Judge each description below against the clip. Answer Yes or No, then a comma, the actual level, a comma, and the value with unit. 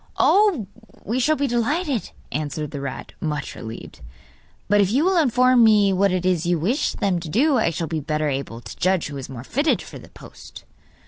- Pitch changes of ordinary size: No, wide, 8.8 semitones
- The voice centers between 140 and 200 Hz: Yes, high, 190 Hz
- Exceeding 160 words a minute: Yes, fast, 205 wpm